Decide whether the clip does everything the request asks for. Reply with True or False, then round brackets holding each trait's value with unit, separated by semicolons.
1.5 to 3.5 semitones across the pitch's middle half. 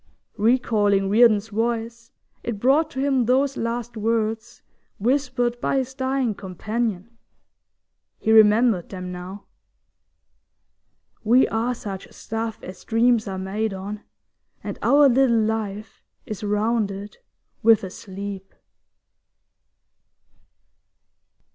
True (3.0 semitones)